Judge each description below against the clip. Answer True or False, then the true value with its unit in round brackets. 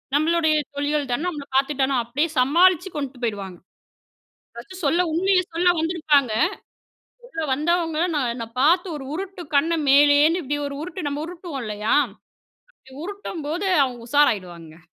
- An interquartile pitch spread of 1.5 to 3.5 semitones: False (4.5 semitones)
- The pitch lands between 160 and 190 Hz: False (295 Hz)